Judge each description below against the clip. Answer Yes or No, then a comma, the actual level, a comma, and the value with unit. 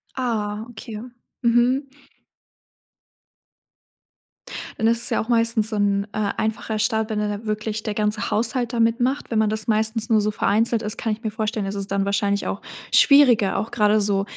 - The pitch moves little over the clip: Yes, narrow, 1.7 semitones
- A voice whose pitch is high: Yes, high, 220 Hz